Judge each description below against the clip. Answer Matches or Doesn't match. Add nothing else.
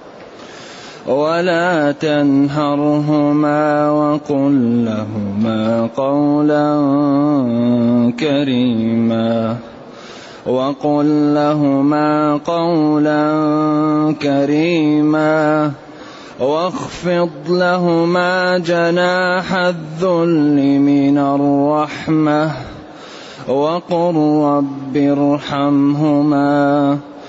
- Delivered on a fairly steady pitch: Matches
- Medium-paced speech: Doesn't match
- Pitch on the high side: Doesn't match